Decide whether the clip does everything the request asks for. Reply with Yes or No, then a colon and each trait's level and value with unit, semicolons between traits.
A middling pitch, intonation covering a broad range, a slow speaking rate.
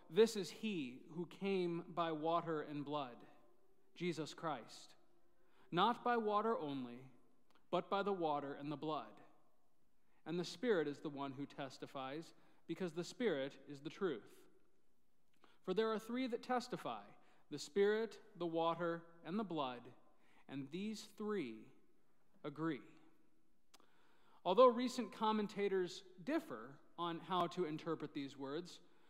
Yes: medium, 170 Hz; wide, 5.8 semitones; slow, 130 wpm